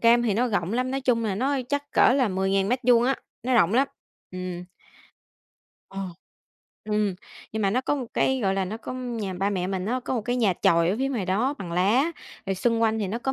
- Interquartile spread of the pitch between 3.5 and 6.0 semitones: Yes, average, 4.7 semitones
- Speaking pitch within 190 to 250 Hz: Yes, high, 225 Hz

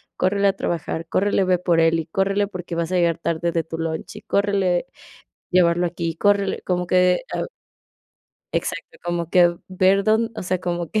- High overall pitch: No, medium, 180 Hz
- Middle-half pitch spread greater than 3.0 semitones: No, narrow, 2.4 semitones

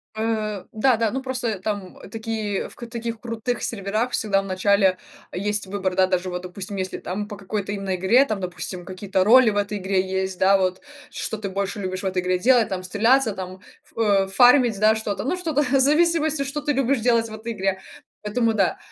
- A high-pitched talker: Yes, high, 210 Hz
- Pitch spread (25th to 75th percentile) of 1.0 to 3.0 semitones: No, average, 3.7 semitones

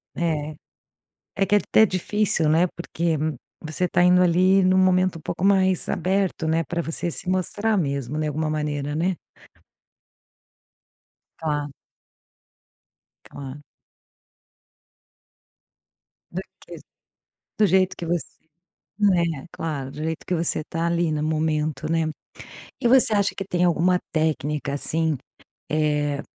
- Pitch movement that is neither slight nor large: Yes, average, 3.2 semitones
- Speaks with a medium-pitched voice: Yes, medium, 165 Hz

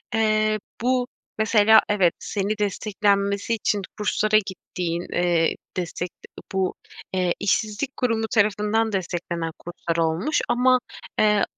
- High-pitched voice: Yes, high, 205 Hz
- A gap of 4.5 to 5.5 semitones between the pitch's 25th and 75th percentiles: No, average, 3.1 semitones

